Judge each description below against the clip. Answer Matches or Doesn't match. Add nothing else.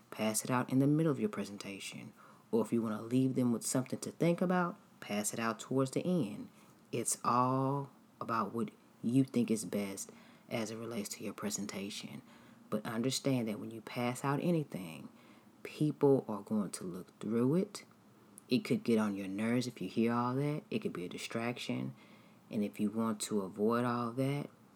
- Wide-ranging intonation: Doesn't match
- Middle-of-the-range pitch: Doesn't match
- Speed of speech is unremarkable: Matches